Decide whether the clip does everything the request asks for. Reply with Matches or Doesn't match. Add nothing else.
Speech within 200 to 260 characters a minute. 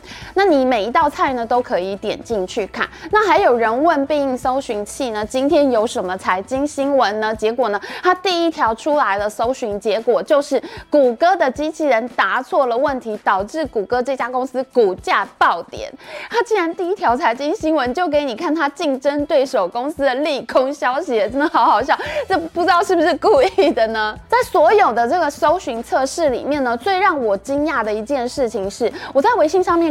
Doesn't match